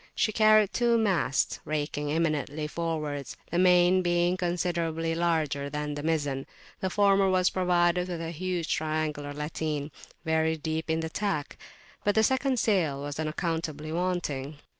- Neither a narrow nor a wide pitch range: Yes, average, 3.2 semitones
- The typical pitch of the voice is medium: Yes, medium, 165 Hz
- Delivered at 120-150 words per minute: Yes, average, 145 wpm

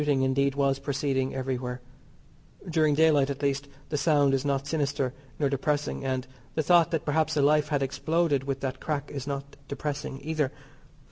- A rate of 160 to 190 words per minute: Yes, average, 175 wpm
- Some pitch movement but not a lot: No, narrow, 1.8 semitones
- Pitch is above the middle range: No, medium, 140 Hz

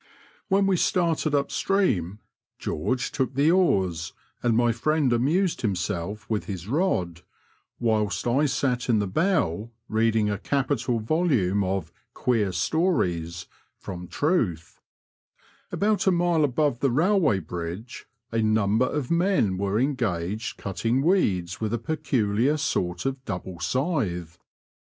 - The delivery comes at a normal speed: No, slow, 130 wpm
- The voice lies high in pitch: No, low, 115 Hz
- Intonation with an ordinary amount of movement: No, wide, 7.6 semitones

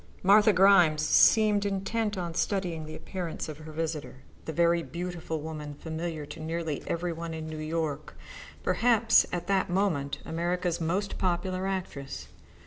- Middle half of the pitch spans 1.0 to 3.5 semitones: Yes, average, 3.2 semitones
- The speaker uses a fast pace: No, average, 155 wpm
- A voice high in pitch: No, medium, 170 Hz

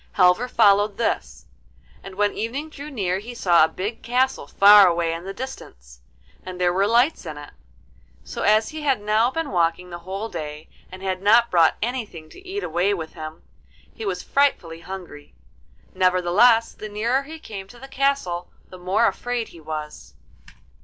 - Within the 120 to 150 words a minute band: No, average, 175 wpm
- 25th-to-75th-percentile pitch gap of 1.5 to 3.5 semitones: No, wide, 5.6 semitones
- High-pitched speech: Yes, high, 200 Hz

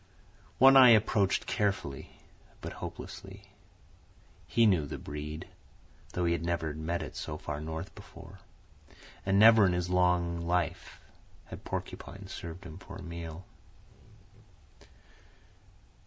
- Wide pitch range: No, average, 3.2 semitones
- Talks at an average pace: No, slow, 125 wpm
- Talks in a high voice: No, very low, 85 Hz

